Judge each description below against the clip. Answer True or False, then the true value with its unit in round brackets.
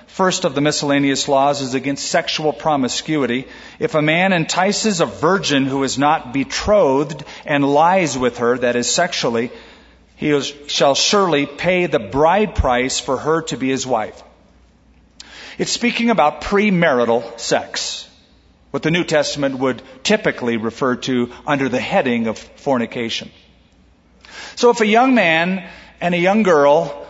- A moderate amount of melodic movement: True (4.7 semitones)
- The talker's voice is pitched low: False (145 Hz)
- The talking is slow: False (145 wpm)